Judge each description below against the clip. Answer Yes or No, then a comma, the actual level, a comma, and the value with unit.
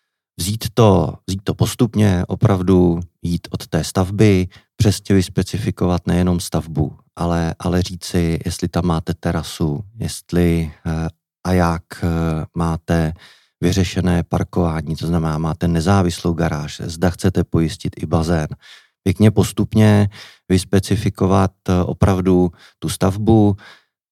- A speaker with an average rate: No, slow, 110 wpm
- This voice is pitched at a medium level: No, very low, 90 Hz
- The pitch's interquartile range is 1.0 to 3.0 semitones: Yes, narrow, 2.6 semitones